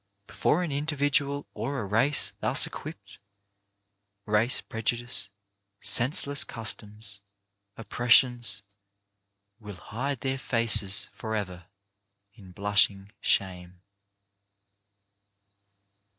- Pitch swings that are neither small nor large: Yes, average, 4.8 semitones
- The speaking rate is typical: No, slow, 80 wpm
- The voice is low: Yes, low, 115 Hz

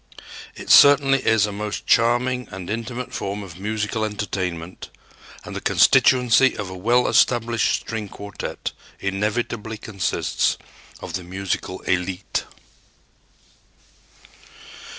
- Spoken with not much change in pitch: No, average, 3.5 semitones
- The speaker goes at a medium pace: No, slow, 110 wpm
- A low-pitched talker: Yes, low, 105 Hz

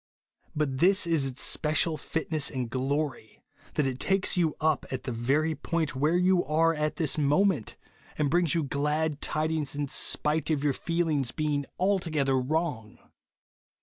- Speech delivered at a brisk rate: No, average, 160 wpm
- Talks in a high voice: No, medium, 150 Hz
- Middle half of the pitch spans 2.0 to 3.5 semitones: Yes, average, 2.9 semitones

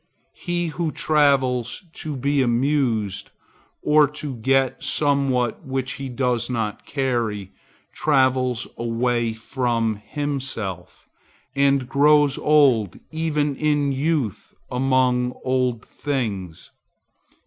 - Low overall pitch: Yes, low, 130 Hz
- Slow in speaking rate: Yes, slow, 95 wpm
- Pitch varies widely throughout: No, average, 3.4 semitones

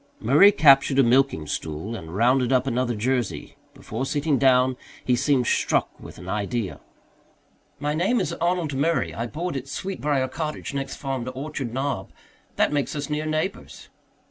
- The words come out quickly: No, average, 165 wpm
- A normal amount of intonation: Yes, average, 3.8 semitones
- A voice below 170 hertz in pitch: Yes, low, 135 Hz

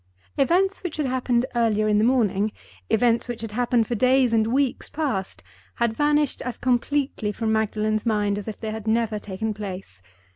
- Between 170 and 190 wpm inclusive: Yes, average, 180 wpm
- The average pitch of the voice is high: Yes, high, 225 Hz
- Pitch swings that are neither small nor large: Yes, average, 3.0 semitones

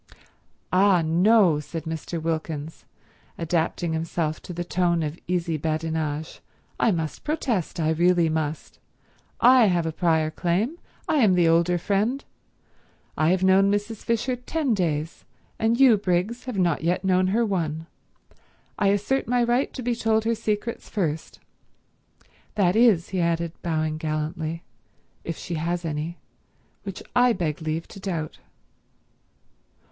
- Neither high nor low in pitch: Yes, medium, 175 Hz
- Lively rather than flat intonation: No, average, 4.6 semitones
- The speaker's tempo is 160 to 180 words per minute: No, average, 140 wpm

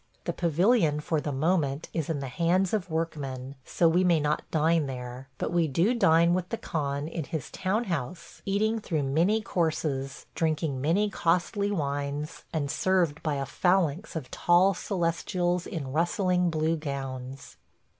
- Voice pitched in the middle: Yes, medium, 165 Hz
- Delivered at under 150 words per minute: No, average, 160 wpm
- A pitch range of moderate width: Yes, average, 4.0 semitones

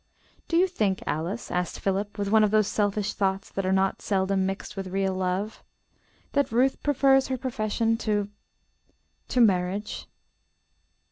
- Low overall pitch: No, high, 205 Hz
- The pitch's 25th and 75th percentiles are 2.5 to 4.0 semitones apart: Yes, average, 2.8 semitones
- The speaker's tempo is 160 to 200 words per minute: No, average, 150 wpm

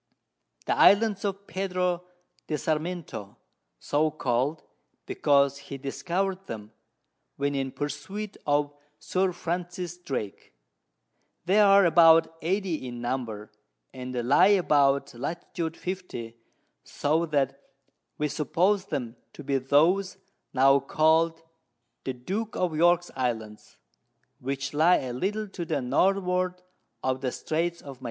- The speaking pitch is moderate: Yes, medium, 155 Hz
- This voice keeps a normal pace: No, slow, 120 wpm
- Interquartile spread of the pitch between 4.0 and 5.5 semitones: Yes, average, 4.9 semitones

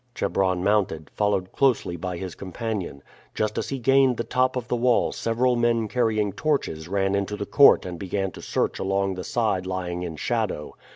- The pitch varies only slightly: No, average, 4.3 semitones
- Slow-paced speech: No, average, 185 wpm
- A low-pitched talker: Yes, low, 100 Hz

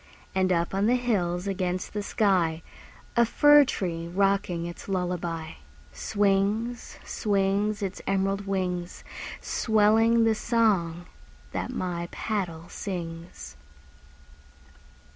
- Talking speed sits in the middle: No, slow, 105 wpm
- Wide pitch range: No, average, 3.4 semitones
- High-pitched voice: Yes, high, 195 Hz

